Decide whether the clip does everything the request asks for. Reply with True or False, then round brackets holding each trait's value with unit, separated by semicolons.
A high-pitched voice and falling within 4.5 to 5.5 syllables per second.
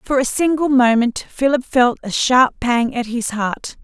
False (250 Hz; 4.2 syllables/s)